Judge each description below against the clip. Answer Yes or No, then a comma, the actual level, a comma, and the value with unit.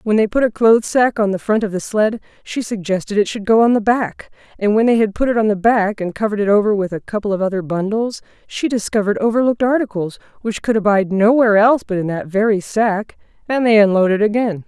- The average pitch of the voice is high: Yes, high, 210 Hz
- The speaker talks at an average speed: No, fast, 235 wpm